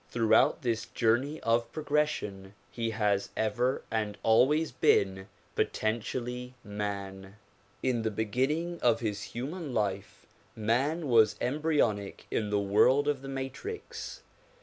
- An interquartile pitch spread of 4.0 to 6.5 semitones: Yes, average, 4.6 semitones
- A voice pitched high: No, low, 115 Hz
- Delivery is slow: Yes, slow, 125 wpm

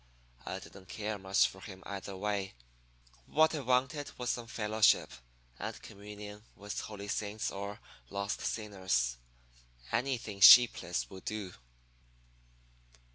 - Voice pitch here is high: No, low, 105 Hz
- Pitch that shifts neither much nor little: No, narrow, 2.2 semitones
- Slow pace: Yes, slow, 120 wpm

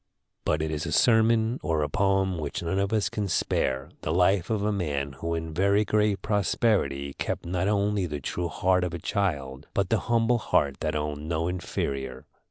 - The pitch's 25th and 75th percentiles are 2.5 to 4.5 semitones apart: No, average, 5.1 semitones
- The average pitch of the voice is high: No, very low, 90 Hz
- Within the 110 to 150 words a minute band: No, average, 195 wpm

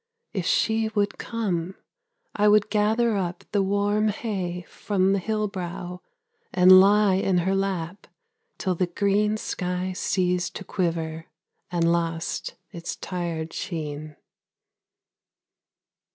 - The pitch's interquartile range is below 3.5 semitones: Yes, average, 3.0 semitones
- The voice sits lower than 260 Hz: Yes, medium, 185 Hz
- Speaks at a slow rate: Yes, slow, 120 wpm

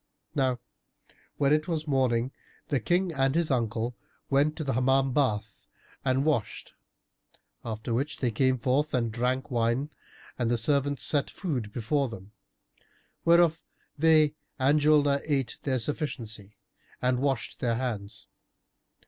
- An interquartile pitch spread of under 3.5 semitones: No, average, 3.8 semitones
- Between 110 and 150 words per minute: Yes, slow, 135 wpm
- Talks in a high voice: No, low, 130 Hz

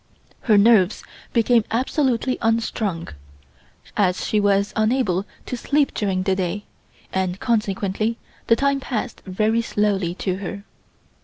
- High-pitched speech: Yes, high, 210 Hz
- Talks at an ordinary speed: No, slow, 125 wpm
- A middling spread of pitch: Yes, average, 3.3 semitones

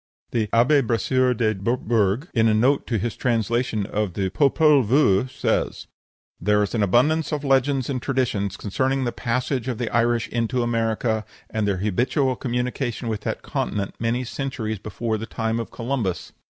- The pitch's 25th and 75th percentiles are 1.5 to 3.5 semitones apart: Yes, average, 3.0 semitones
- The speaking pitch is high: No, low, 120 Hz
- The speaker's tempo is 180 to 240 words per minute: No, average, 165 wpm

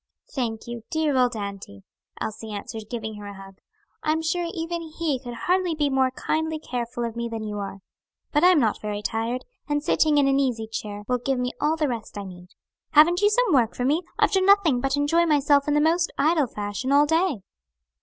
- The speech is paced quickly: Yes, fast, 220 wpm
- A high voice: Yes, very high, 265 Hz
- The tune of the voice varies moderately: No, wide, 6.1 semitones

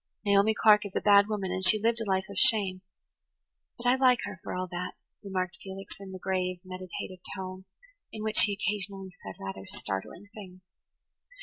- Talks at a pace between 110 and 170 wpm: No, average, 195 wpm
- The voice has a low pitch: No, high, 190 Hz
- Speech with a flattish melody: Yes, narrow, 2.2 semitones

